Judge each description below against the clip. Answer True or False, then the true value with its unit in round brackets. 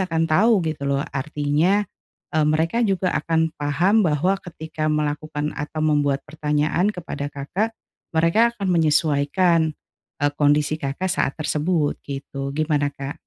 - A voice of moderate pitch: True (155 Hz)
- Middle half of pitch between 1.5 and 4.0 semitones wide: True (3.3 semitones)